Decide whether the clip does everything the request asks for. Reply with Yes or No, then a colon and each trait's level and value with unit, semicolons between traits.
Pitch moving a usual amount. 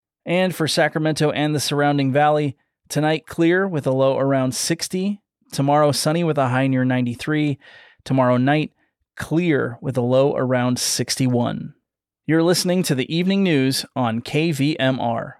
Yes: average, 3.4 semitones